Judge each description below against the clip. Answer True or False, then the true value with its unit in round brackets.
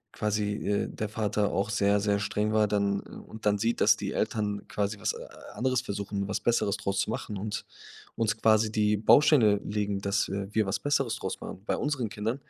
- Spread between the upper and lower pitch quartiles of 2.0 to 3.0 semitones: False (1.4 semitones)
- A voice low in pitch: True (105 Hz)